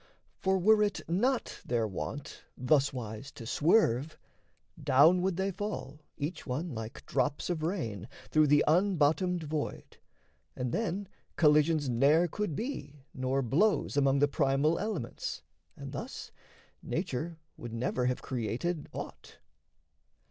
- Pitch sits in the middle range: Yes, medium, 150 Hz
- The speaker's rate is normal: No, slow, 125 wpm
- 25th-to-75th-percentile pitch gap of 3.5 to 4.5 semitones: No, wide, 5.4 semitones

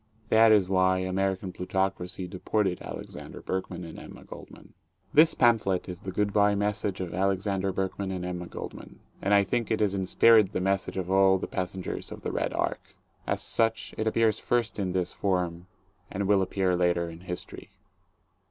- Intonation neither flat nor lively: No, narrow, 2.0 semitones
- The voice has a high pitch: No, very low, 95 Hz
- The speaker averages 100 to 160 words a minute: No, average, 180 wpm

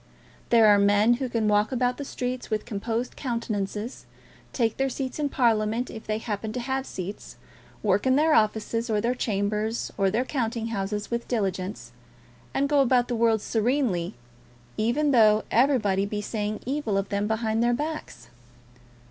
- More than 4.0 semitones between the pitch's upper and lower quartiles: No, average, 3.1 semitones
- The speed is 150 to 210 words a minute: Yes, average, 165 wpm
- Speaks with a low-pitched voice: No, high, 225 Hz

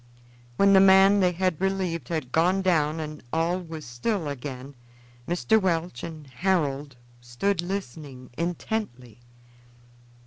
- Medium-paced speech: No, slow, 125 wpm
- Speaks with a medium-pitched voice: Yes, medium, 165 Hz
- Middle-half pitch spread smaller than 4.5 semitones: No, average, 5.0 semitones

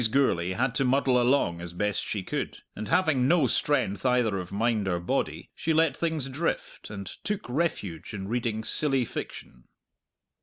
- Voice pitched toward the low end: Yes, low, 125 Hz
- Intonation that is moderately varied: No, wide, 6.1 semitones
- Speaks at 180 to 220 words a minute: No, average, 165 wpm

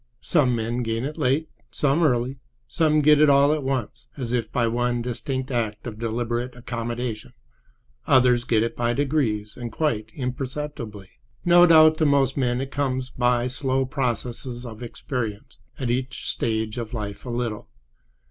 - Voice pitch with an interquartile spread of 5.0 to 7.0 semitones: No, average, 2.7 semitones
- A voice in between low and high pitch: No, low, 125 Hz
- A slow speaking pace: No, average, 155 wpm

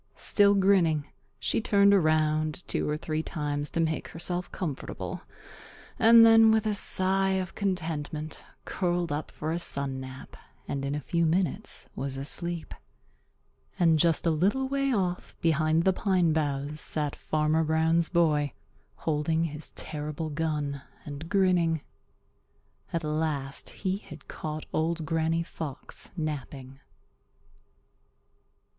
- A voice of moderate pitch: Yes, medium, 160 Hz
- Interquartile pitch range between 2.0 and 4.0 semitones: Yes, average, 3.2 semitones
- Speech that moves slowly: Yes, slow, 130 wpm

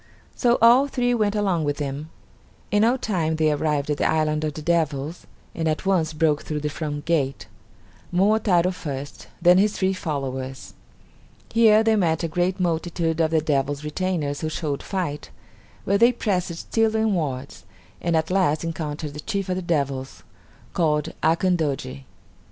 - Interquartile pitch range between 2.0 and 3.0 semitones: No, average, 4.1 semitones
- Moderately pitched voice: Yes, medium, 165 Hz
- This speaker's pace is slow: No, average, 165 wpm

